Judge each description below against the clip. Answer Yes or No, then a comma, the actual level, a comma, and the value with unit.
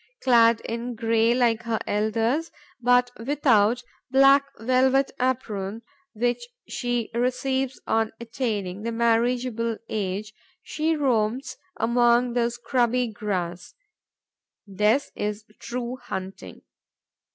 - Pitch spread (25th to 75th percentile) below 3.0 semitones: Yes, narrow, 2.4 semitones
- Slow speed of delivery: Yes, slow, 105 wpm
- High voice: Yes, high, 235 Hz